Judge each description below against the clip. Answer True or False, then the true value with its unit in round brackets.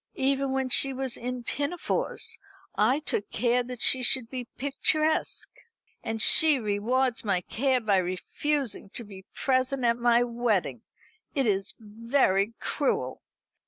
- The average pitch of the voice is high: True (245 Hz)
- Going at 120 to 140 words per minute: True (135 wpm)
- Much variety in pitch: False (3.5 semitones)